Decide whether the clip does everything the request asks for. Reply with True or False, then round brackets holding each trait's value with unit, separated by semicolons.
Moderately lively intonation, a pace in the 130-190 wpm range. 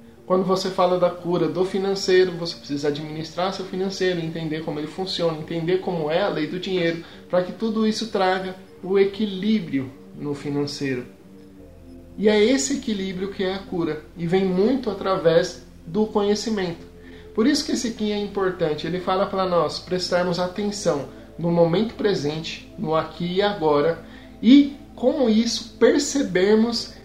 True (4.3 semitones; 155 wpm)